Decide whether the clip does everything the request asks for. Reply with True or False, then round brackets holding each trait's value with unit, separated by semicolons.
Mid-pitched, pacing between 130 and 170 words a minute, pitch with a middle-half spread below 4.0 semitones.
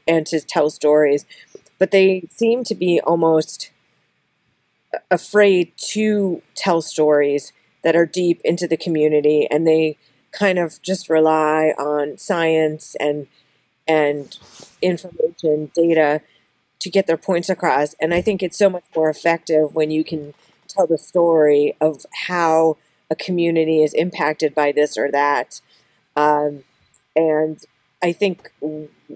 True (160 Hz; 135 wpm; 2.7 semitones)